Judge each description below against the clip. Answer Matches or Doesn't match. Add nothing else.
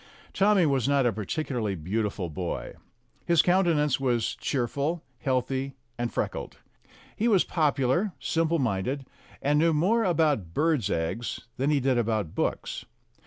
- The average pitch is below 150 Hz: Matches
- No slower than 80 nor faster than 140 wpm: Matches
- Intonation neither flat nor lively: Doesn't match